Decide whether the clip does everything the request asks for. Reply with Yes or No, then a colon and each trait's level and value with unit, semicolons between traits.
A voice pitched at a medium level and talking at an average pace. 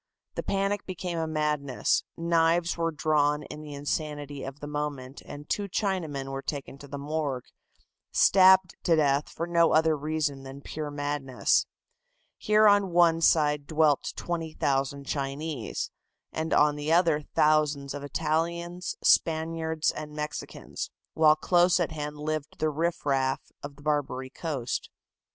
Yes: medium, 150 Hz; average, 145 wpm